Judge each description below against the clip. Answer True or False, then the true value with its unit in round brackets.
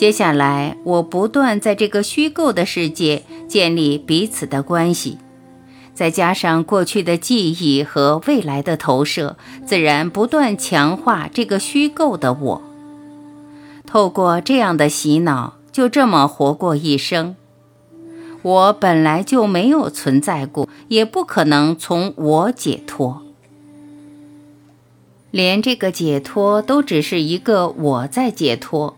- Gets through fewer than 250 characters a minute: True (190 characters per minute)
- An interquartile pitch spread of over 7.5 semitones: False (6.7 semitones)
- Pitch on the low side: False (170 Hz)